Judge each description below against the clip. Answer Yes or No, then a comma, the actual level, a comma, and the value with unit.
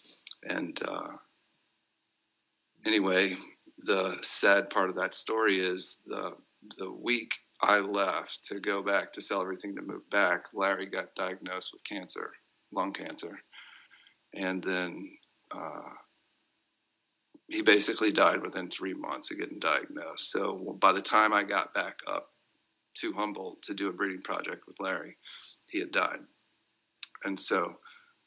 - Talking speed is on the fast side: No, average, 140 wpm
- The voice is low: No, very high, 310 Hz